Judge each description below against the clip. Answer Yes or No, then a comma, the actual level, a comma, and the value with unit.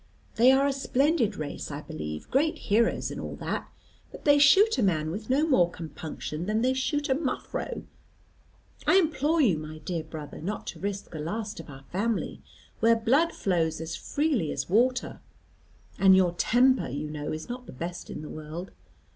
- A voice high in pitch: Yes, high, 205 Hz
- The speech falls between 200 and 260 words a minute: No, average, 185 wpm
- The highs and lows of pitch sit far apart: Yes, wide, 8.7 semitones